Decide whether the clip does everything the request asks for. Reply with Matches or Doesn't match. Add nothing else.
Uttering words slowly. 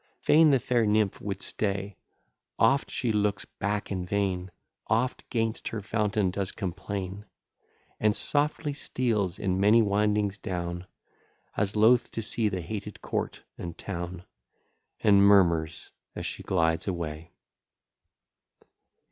Matches